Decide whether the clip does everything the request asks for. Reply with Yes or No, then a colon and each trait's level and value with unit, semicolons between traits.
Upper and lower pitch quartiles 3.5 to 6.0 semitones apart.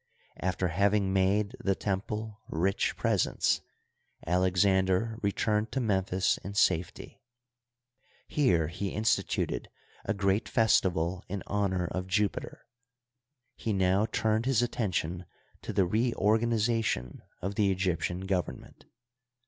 No: narrow, 2.6 semitones